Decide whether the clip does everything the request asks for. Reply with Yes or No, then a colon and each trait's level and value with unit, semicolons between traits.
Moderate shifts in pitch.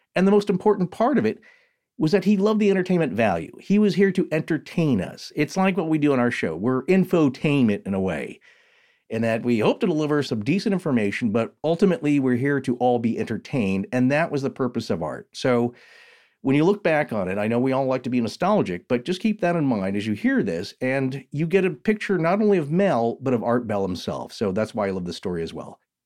No: wide, 7.7 semitones